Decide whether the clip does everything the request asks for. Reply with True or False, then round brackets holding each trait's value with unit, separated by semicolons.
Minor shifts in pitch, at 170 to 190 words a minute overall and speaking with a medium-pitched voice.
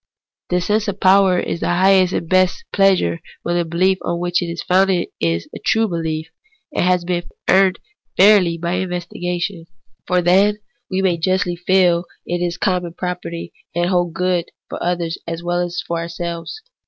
True (1.6 semitones; 180 wpm; 180 Hz)